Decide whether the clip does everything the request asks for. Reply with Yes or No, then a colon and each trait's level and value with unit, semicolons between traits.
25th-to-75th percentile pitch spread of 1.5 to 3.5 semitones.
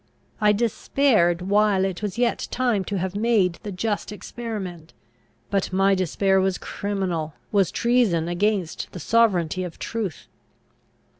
Yes: average, 3.0 semitones